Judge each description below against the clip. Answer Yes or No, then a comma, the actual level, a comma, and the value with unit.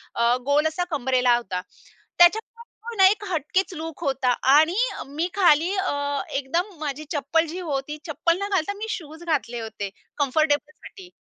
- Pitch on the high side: Yes, very high, 310 Hz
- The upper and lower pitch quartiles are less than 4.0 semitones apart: No, average, 4.4 semitones